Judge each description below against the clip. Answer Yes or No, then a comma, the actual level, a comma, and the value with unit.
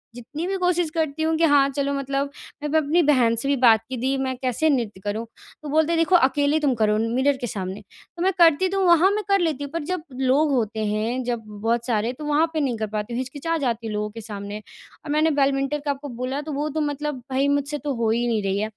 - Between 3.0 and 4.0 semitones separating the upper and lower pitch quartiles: No, average, 4.7 semitones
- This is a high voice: Yes, very high, 275 Hz